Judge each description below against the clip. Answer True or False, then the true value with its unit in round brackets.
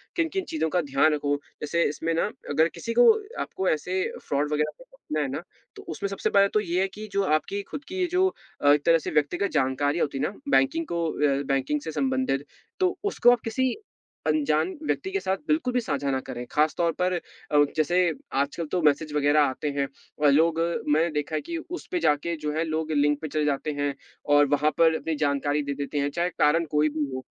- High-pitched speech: False (155 Hz)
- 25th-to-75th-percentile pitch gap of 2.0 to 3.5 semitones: False (4.6 semitones)